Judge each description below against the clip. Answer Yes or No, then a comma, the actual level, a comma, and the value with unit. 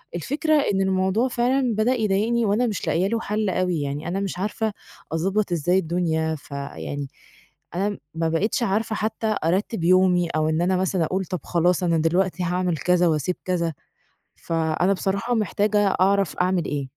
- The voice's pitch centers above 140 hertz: Yes, medium, 185 Hz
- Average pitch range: Yes, average, 3.8 semitones